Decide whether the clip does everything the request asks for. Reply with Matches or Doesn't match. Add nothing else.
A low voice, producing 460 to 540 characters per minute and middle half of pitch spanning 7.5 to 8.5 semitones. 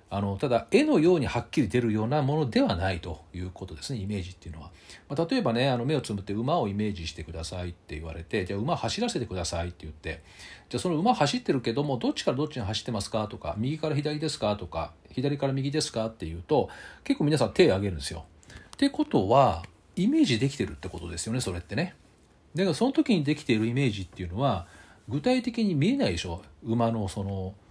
Matches